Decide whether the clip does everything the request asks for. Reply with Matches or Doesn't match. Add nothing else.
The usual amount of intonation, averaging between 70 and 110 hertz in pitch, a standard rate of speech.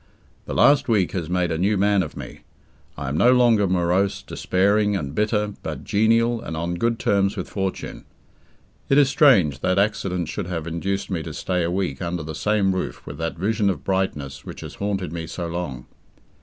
Matches